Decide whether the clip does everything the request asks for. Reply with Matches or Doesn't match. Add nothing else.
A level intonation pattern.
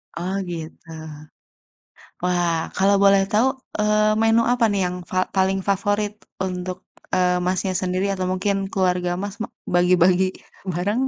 Matches